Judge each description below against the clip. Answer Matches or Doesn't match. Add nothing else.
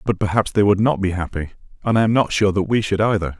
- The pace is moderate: Doesn't match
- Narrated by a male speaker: Matches